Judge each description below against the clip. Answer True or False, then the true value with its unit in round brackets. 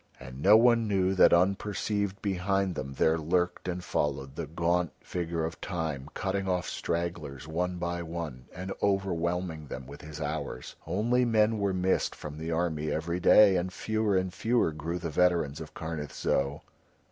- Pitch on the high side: False (85 Hz)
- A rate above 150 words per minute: True (170 wpm)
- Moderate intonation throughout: True (3.4 semitones)